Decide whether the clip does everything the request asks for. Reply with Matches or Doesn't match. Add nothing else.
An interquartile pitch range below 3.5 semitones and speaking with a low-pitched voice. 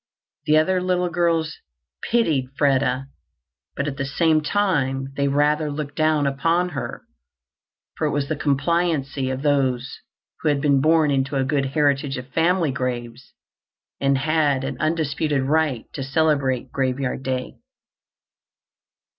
Doesn't match